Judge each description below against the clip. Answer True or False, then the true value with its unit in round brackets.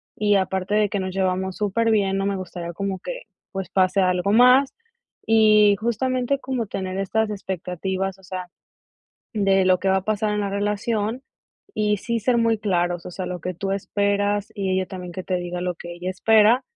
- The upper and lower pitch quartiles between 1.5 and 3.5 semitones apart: True (2.4 semitones)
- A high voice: True (195 Hz)